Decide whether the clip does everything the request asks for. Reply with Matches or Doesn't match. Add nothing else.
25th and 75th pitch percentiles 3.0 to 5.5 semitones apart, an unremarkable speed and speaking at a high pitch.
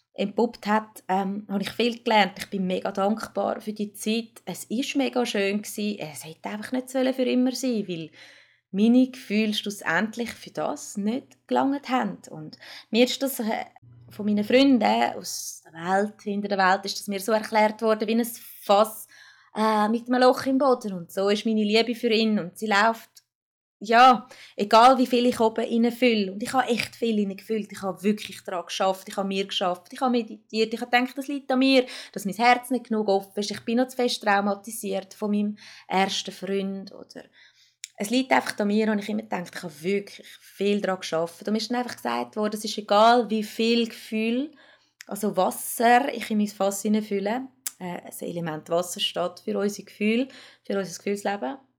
Doesn't match